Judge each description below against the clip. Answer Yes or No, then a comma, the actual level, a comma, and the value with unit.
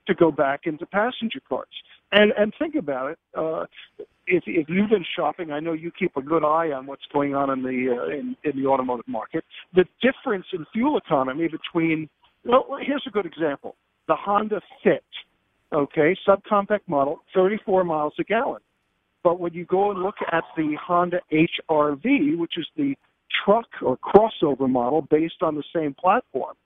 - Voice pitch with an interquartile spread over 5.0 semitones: Yes, wide, 5.6 semitones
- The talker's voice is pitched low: No, medium, 175 Hz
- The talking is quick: No, average, 180 wpm